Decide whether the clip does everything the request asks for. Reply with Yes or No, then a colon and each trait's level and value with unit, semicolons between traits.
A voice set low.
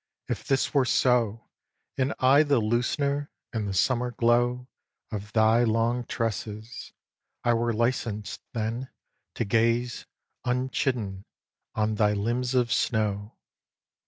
Yes: low, 120 Hz